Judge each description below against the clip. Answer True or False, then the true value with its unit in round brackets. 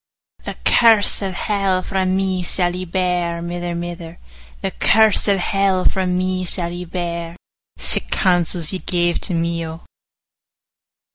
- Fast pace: False (150 wpm)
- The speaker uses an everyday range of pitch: False (1.6 semitones)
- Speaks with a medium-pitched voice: True (180 Hz)